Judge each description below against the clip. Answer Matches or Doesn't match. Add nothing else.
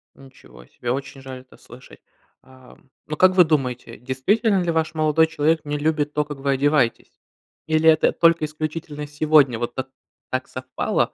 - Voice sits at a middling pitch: Matches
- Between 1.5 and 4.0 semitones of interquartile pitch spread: Matches